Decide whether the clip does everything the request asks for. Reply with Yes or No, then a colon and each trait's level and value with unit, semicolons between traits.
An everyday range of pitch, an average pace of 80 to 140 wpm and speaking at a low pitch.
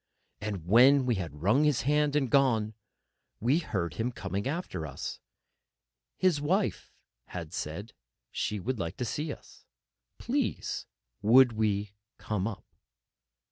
No: wide, 6.2 semitones; slow, 135 wpm; low, 115 Hz